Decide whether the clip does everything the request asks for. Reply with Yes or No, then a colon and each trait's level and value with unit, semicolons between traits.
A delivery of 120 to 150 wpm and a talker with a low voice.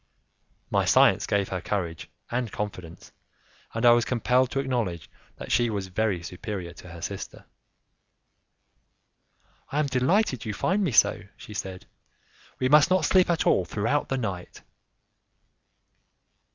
Yes: average, 140 wpm; low, 110 Hz